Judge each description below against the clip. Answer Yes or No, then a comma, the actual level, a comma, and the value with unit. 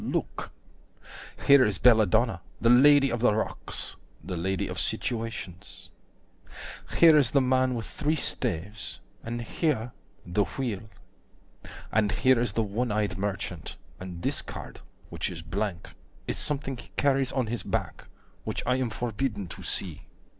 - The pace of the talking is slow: No, average, 150 wpm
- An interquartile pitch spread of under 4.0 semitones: No, average, 4.7 semitones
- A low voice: Yes, low, 115 Hz